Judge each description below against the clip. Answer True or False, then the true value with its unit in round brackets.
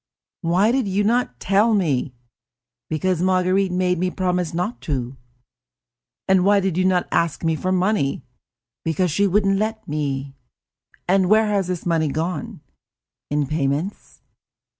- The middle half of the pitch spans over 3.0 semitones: True (3.7 semitones)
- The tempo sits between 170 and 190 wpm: False (145 wpm)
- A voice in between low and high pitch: True (180 Hz)